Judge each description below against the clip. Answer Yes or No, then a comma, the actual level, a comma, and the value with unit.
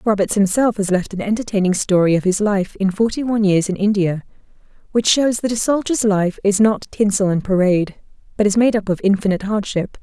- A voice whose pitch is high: Yes, high, 200 Hz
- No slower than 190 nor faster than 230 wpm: Yes, fast, 205 wpm